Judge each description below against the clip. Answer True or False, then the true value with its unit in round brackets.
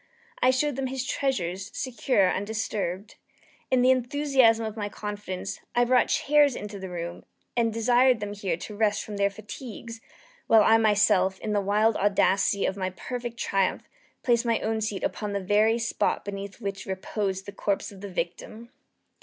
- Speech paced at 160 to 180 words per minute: True (170 wpm)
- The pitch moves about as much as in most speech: True (3.1 semitones)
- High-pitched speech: True (210 Hz)